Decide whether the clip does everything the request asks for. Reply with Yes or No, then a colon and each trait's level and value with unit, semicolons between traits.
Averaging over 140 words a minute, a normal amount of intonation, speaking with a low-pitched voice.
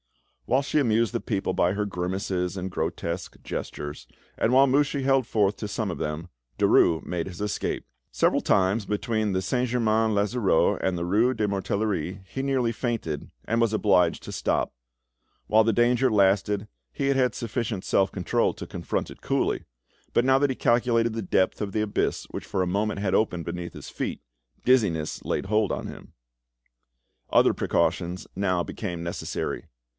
Yes: average, 175 wpm; average, 4.1 semitones; low, 105 Hz